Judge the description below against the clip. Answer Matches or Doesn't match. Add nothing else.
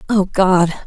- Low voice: Doesn't match